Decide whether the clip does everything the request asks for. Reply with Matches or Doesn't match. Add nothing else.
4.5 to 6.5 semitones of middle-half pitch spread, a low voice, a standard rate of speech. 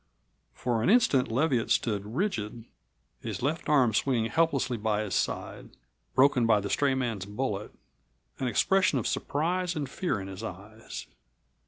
Matches